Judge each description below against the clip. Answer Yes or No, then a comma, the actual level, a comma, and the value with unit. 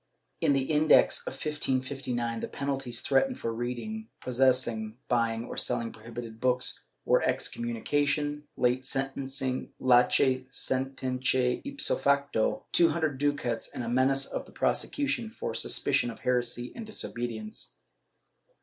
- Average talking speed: No, slow, 120 wpm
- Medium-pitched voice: No, low, 130 Hz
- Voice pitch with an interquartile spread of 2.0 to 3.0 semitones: Yes, average, 2.7 semitones